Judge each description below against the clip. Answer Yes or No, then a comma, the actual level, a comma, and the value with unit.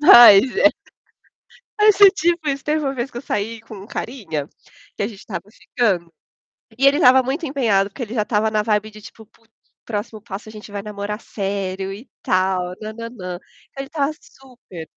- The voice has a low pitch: No, high, 220 Hz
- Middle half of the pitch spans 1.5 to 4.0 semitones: No, average, 4.8 semitones